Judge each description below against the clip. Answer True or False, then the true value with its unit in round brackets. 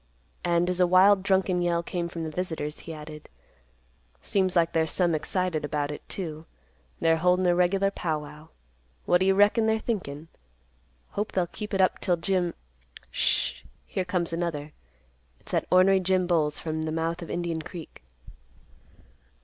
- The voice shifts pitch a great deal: False (2.7 semitones)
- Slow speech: False (165 wpm)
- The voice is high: False (175 Hz)